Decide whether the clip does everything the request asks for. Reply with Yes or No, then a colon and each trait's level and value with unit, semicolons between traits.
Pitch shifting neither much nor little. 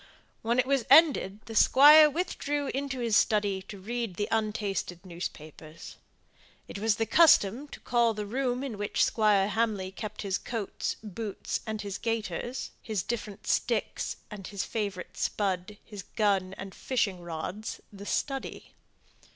Yes: average, 3.6 semitones